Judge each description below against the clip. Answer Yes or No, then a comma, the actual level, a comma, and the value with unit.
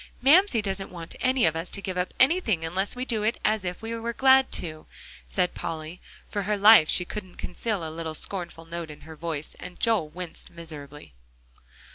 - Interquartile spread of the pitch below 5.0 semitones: No, average, 5.3 semitones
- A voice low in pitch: No, medium, 180 Hz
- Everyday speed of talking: Yes, average, 195 wpm